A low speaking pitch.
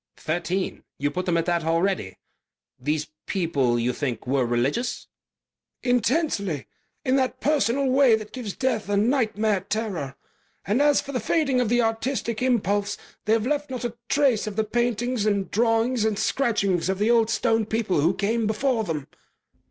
No: high, 220 Hz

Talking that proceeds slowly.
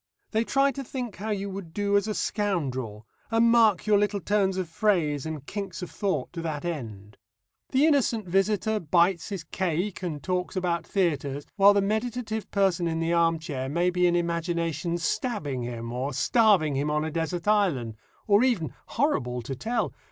No: average, 180 wpm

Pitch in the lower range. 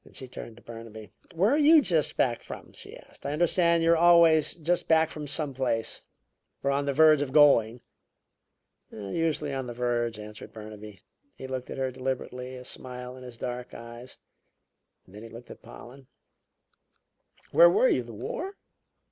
Yes: low, 130 Hz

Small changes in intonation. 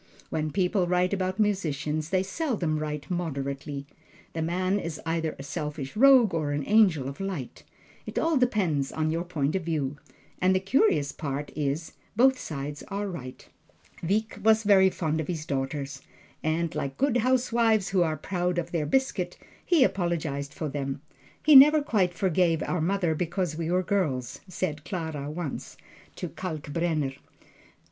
No: average, 4.6 semitones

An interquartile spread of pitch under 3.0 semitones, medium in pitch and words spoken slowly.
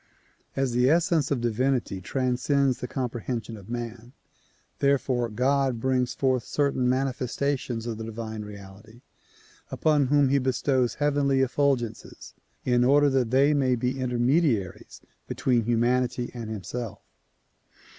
No: narrow, 2.5 semitones; low, 125 Hz; slow, 125 wpm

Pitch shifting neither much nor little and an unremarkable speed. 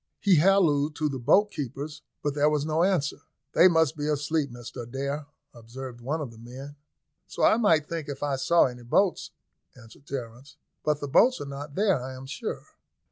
Yes: average, 3.2 semitones; average, 190 wpm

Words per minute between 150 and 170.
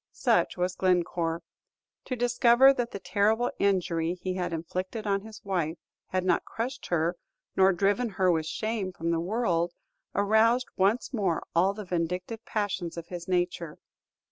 Yes: average, 155 wpm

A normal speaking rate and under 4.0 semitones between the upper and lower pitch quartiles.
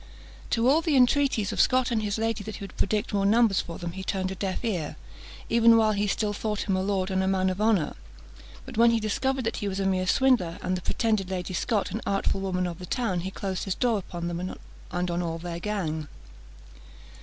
No: fast, 235 wpm; average, 3.4 semitones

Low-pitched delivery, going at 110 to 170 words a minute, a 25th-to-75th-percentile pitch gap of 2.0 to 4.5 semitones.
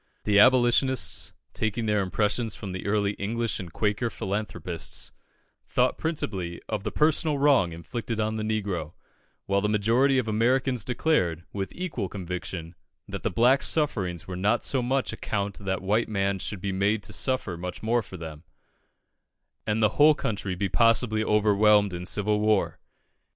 Yes: low, 105 Hz; average, 160 wpm; average, 3.5 semitones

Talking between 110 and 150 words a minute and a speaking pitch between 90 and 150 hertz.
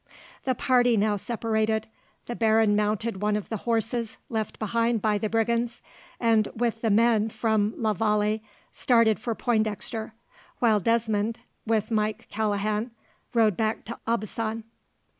No: average, 140 wpm; high, 220 Hz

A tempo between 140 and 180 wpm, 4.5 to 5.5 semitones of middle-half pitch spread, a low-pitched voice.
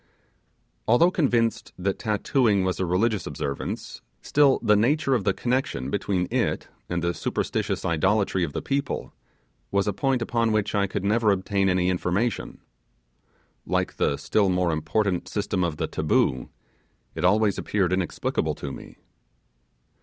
No: average, 145 wpm; average, 4.1 semitones; low, 100 Hz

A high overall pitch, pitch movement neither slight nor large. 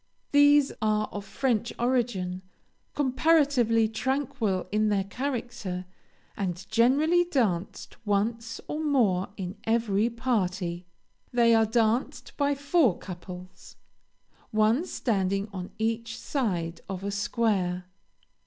Yes: high, 220 Hz; average, 4.6 semitones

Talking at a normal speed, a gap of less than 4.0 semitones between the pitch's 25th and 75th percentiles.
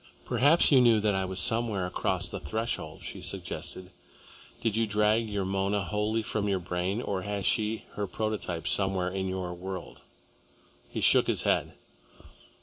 Yes: average, 160 wpm; average, 2.7 semitones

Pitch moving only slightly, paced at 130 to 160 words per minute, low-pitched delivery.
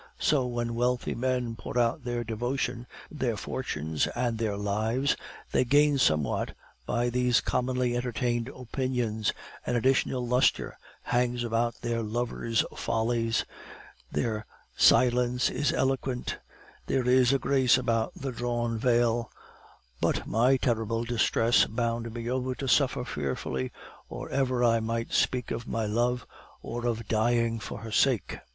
Yes: narrow, 1.6 semitones; slow, 135 wpm; low, 120 Hz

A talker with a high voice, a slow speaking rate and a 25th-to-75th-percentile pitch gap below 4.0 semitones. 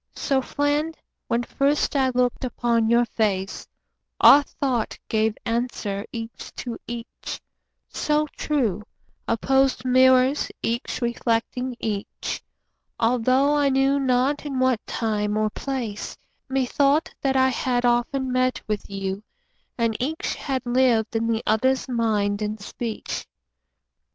Yes: high, 245 Hz; slow, 125 wpm; average, 3.0 semitones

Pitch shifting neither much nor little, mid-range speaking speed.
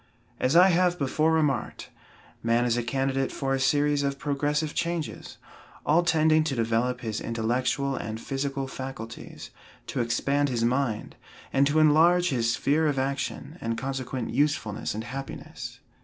Yes: average, 3.5 semitones; average, 150 wpm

